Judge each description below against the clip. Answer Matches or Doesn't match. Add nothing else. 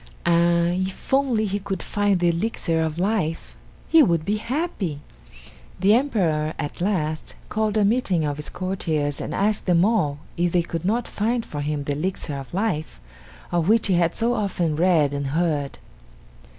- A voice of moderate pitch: Matches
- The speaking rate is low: Doesn't match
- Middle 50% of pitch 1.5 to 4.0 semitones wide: Doesn't match